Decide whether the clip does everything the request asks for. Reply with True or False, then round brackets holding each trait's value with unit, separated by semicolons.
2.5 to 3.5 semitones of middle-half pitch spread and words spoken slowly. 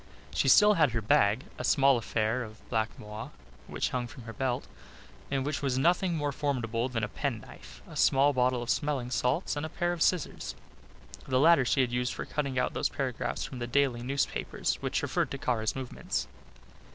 False (3.2 semitones; 195 wpm)